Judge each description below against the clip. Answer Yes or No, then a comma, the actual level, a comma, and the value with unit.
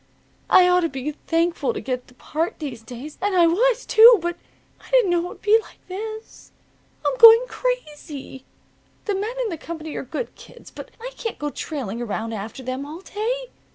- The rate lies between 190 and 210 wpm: Yes, average, 195 wpm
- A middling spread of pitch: No, wide, 8.0 semitones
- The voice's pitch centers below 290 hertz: No, very high, 345 Hz